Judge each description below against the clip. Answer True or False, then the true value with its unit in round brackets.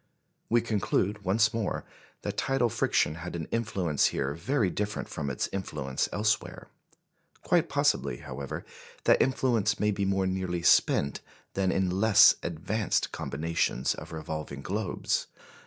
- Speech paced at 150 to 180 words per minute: False (135 wpm)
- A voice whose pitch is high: False (95 Hz)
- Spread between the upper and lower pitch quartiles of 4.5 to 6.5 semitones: True (5.0 semitones)